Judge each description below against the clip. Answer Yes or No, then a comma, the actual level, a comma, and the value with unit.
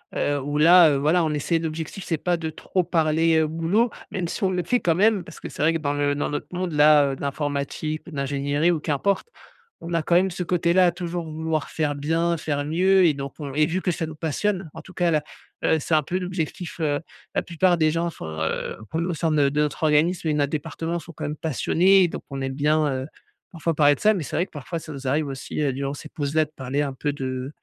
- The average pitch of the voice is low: No, medium, 155 Hz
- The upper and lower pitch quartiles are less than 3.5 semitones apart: Yes, average, 3.0 semitones